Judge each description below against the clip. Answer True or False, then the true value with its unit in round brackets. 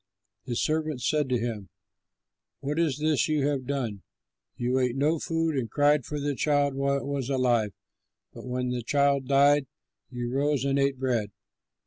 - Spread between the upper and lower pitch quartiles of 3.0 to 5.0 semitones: False (2.6 semitones)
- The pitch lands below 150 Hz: True (140 Hz)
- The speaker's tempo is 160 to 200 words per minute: True (170 wpm)